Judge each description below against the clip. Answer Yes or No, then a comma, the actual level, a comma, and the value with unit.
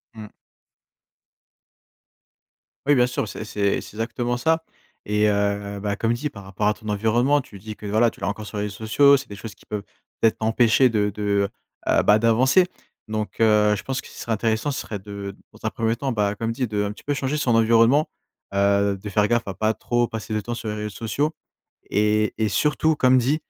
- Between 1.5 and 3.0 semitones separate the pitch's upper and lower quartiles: Yes, average, 2.7 semitones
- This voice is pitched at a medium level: No, low, 110 Hz